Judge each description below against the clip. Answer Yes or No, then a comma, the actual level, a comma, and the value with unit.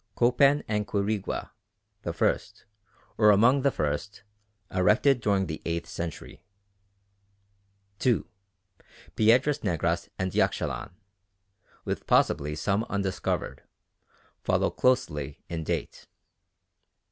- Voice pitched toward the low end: Yes, low, 100 Hz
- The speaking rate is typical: No, slow, 95 wpm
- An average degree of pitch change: No, wide, 6.0 semitones